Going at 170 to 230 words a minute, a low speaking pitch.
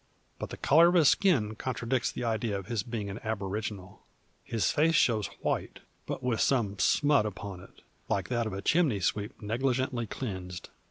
Yes: average, 175 wpm; low, 115 Hz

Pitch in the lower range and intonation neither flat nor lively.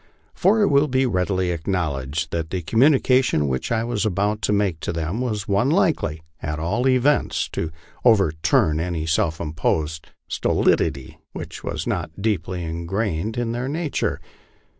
No: very low, 95 Hz; wide, 7.0 semitones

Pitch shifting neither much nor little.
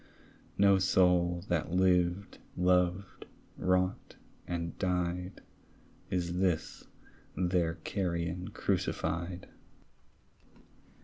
No: narrow, 1.1 semitones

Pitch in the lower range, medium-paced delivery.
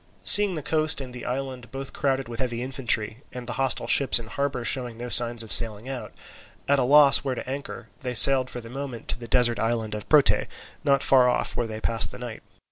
No: low, 125 Hz; fast, 225 wpm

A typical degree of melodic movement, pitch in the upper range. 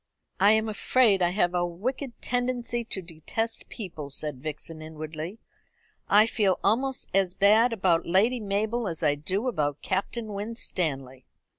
No: wide, 5.7 semitones; high, 195 Hz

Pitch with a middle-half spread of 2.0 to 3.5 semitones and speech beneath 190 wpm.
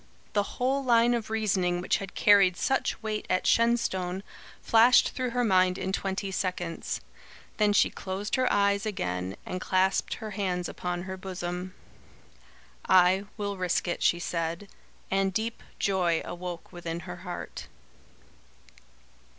Yes: average, 2.9 semitones; average, 140 wpm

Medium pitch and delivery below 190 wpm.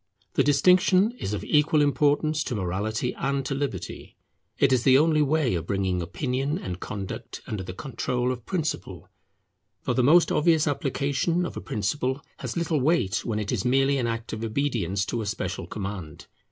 No: low, 130 Hz; average, 180 wpm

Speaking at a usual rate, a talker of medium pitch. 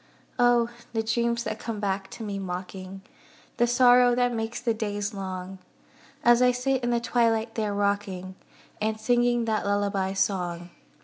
No: average, 160 wpm; high, 220 Hz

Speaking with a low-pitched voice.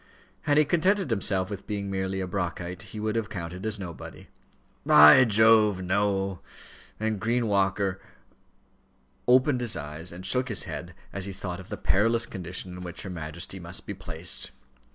Yes: very low, 95 Hz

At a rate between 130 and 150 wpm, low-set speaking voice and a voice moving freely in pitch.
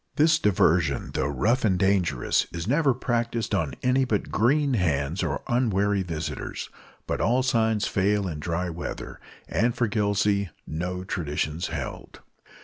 Yes: average, 140 wpm; low, 100 Hz; wide, 5.9 semitones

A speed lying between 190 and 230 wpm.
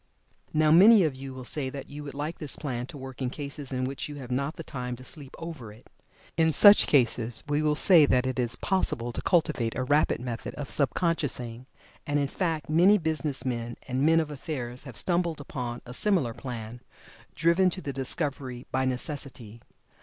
Yes: average, 200 wpm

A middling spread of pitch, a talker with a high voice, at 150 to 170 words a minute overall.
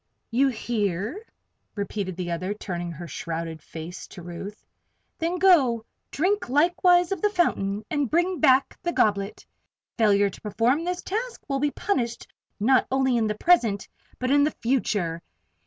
No: wide, 8.1 semitones; high, 235 Hz; average, 155 wpm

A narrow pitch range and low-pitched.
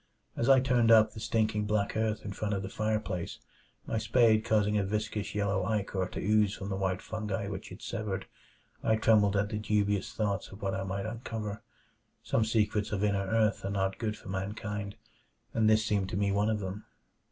Yes: narrow, 1.7 semitones; low, 105 Hz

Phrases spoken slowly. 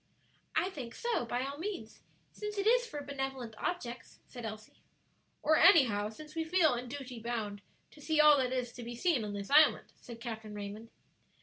No: average, 190 wpm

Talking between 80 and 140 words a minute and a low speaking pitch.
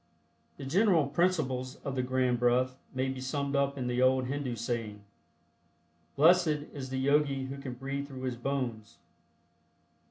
No: average, 155 wpm; low, 130 Hz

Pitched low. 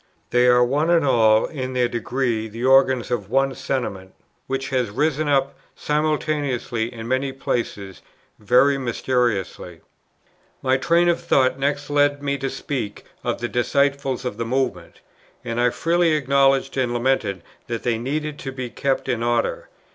Yes: low, 130 Hz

